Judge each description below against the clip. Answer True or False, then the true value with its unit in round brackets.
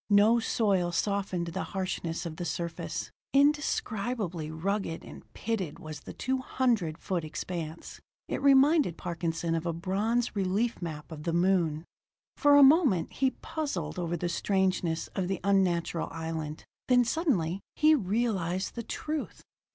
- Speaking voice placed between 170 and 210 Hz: True (185 Hz)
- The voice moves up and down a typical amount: False (5.8 semitones)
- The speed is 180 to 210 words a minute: False (145 wpm)